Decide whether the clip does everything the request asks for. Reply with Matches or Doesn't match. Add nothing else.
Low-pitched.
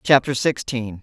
Matches